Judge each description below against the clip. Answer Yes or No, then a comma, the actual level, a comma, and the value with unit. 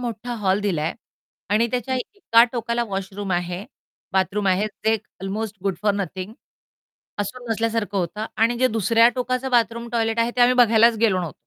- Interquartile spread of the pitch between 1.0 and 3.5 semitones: Yes, average, 3.2 semitones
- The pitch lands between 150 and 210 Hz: No, high, 220 Hz